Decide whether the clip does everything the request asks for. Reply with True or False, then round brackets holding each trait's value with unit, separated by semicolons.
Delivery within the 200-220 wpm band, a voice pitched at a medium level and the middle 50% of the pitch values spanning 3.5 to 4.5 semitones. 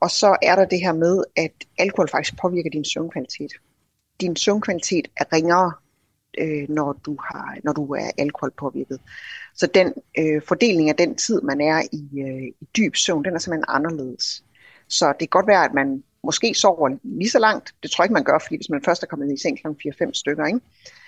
True (215 wpm; 155 Hz; 4.0 semitones)